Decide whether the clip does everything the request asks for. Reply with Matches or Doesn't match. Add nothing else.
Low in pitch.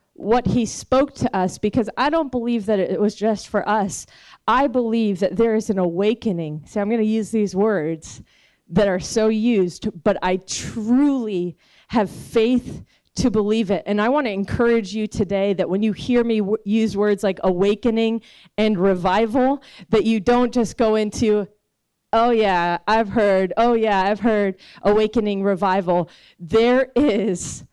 Doesn't match